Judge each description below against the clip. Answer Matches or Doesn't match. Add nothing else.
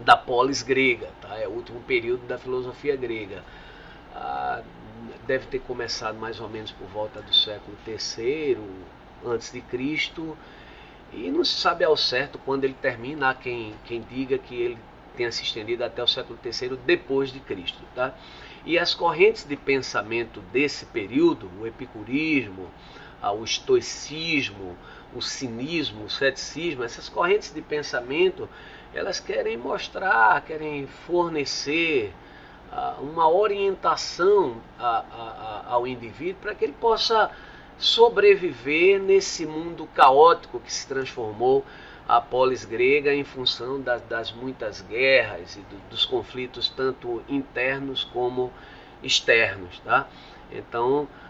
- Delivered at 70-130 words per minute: Matches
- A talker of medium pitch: Matches